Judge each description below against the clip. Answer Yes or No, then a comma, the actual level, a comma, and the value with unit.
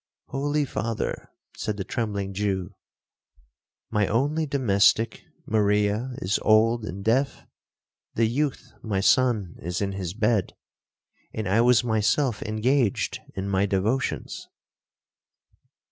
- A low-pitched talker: Yes, low, 110 Hz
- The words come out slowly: Yes, slow, 115 wpm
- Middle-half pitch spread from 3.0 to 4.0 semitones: Yes, average, 3.7 semitones